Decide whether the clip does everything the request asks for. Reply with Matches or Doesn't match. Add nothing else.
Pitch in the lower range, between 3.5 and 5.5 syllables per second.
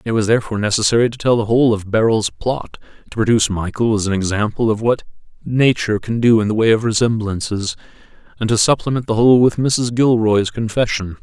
Doesn't match